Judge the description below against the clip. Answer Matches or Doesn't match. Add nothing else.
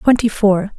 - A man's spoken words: Doesn't match